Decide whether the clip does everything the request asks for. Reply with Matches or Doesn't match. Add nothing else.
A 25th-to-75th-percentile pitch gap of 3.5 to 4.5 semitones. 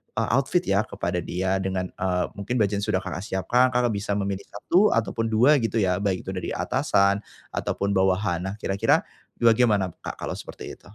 Doesn't match